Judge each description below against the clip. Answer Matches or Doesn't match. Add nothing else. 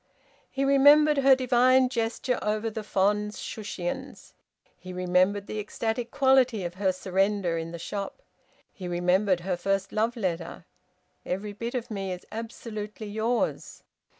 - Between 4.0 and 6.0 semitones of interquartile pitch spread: Matches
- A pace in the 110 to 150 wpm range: Matches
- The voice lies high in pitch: Matches